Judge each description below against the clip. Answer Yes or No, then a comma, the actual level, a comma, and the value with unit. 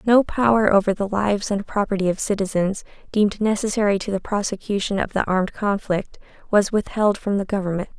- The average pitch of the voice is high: Yes, high, 200 Hz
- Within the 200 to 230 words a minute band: No, average, 175 wpm